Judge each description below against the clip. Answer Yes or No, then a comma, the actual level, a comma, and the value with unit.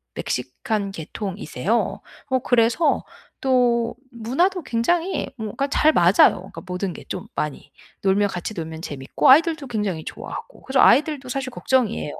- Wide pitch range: Yes, wide, 5.7 semitones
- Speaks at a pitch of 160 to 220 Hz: No, high, 230 Hz